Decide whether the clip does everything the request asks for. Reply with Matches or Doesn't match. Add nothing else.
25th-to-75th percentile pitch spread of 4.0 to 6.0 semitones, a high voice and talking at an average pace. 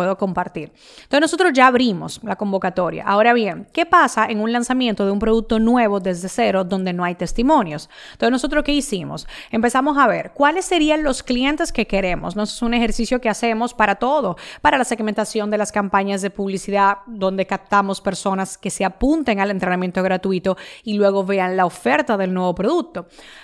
Matches